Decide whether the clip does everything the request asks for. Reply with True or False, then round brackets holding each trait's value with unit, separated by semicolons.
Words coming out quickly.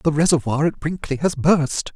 False (185 wpm)